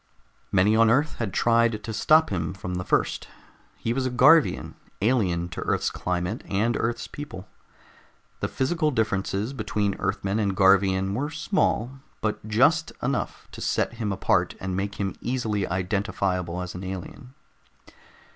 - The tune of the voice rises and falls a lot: No, average, 4.6 semitones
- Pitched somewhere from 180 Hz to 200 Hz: No, low, 105 Hz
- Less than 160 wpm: Yes, average, 150 wpm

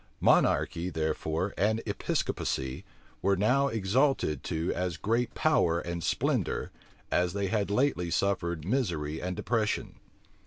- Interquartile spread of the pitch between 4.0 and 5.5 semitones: Yes, average, 4.7 semitones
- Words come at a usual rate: No, slow, 120 wpm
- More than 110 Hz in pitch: No, very low, 95 Hz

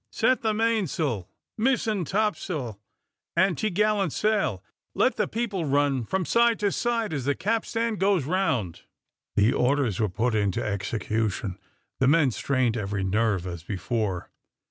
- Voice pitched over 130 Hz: Yes, medium, 140 Hz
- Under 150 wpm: Yes, average, 140 wpm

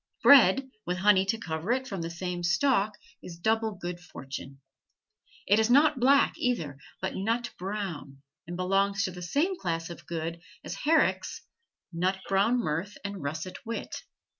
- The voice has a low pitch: No, high, 190 Hz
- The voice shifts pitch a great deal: No, average, 4.7 semitones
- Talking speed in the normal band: Yes, average, 160 wpm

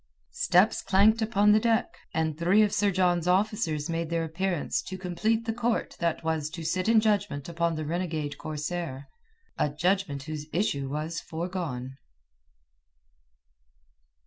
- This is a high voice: No, medium, 175 Hz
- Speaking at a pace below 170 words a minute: Yes, average, 145 wpm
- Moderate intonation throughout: Yes, average, 4.4 semitones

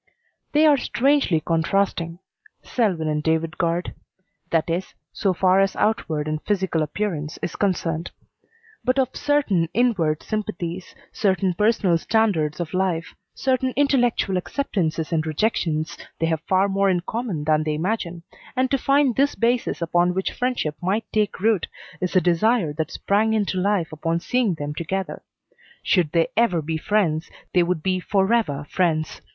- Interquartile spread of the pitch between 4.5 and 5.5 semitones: Yes, average, 5.0 semitones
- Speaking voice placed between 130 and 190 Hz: Yes, medium, 185 Hz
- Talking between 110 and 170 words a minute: Yes, average, 155 wpm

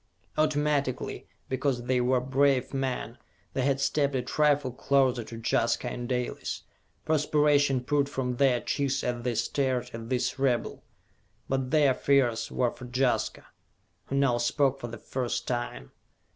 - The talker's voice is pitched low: Yes, low, 130 Hz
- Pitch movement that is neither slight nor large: No, narrow, 2.2 semitones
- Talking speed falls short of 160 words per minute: Yes, average, 145 wpm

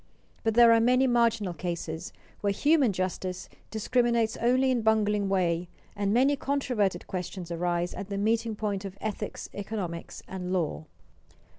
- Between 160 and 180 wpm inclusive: No, average, 150 wpm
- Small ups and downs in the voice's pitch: No, average, 4.2 semitones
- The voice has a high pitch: Yes, high, 205 Hz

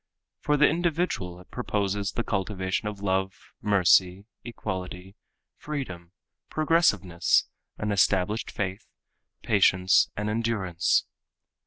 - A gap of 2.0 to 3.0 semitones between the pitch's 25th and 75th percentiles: No, average, 3.6 semitones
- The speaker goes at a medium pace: No, slow, 100 wpm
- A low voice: Yes, low, 100 Hz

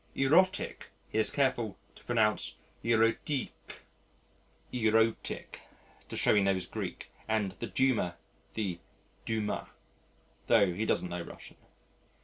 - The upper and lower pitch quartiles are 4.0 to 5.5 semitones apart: No, average, 3.2 semitones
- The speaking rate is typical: No, slow, 110 wpm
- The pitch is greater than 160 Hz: No, low, 110 Hz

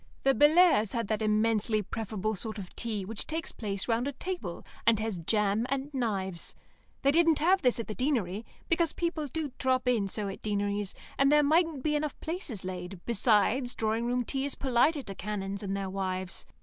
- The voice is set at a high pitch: Yes, high, 230 Hz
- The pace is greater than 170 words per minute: Yes, average, 190 wpm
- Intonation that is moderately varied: No, wide, 5.7 semitones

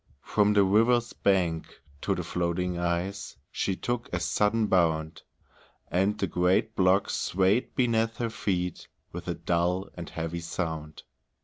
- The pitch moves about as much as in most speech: Yes, average, 3.3 semitones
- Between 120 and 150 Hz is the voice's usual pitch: No, very low, 95 Hz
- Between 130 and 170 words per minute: Yes, average, 140 wpm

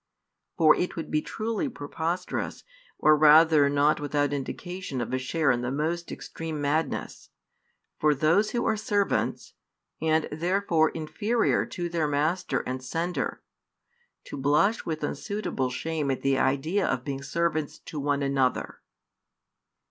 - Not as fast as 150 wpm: Yes, average, 140 wpm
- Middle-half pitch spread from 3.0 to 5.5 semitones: Yes, average, 3.4 semitones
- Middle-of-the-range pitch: Yes, medium, 155 Hz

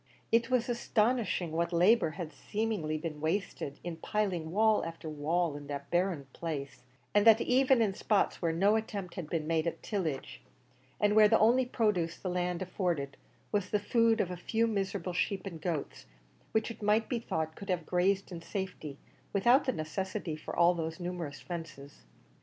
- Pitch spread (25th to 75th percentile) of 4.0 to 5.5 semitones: Yes, average, 4.5 semitones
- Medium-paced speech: Yes, average, 180 wpm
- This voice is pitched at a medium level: Yes, medium, 180 Hz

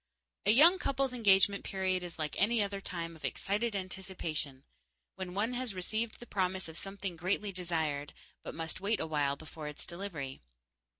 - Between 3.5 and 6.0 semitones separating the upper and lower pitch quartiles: Yes, average, 4.0 semitones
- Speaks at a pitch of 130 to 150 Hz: No, high, 190 Hz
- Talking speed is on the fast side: No, average, 165 wpm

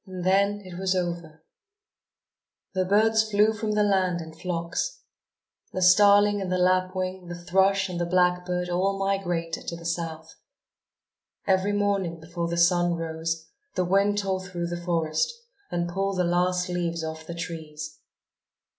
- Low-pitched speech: No, medium, 180 Hz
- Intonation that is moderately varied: No, narrow, 2.3 semitones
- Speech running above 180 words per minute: No, average, 155 wpm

